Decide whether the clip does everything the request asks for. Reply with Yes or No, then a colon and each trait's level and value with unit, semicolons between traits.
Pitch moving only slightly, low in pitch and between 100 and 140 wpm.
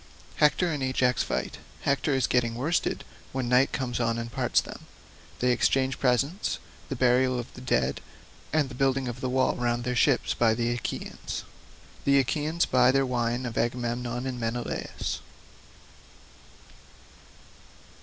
Yes: narrow, 1.9 semitones; low, 125 Hz; slow, 135 wpm